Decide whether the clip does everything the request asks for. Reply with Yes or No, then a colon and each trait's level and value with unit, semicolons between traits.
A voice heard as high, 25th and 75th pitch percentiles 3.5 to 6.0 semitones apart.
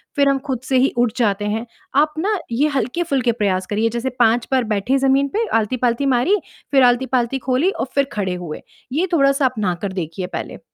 Yes: very high, 255 Hz; average, 4.1 semitones